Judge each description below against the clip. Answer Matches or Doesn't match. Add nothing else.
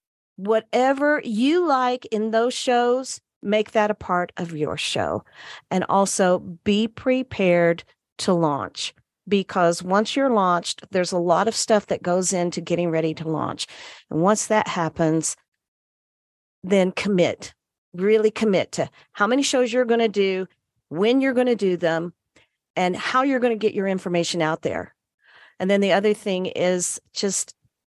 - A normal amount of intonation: Matches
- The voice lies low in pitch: Doesn't match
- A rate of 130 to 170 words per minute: Matches